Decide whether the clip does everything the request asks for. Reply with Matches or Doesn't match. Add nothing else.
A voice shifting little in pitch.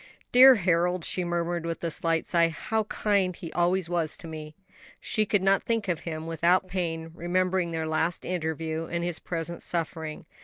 Matches